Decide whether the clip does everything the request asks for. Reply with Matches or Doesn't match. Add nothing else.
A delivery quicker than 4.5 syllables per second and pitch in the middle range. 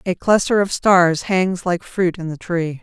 Doesn't match